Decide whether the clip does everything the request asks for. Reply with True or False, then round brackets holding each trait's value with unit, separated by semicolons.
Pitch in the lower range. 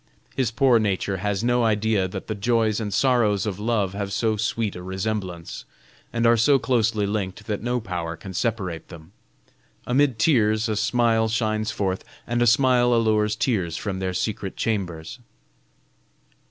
True (110 Hz)